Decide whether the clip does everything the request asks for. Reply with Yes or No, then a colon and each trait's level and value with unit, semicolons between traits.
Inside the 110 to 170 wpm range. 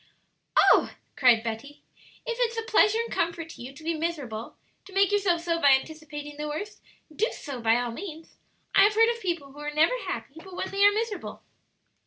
No: fast, 205 wpm